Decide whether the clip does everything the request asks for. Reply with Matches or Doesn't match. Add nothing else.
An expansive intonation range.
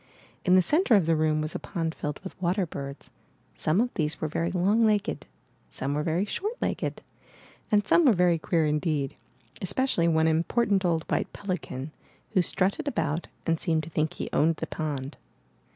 Doesn't match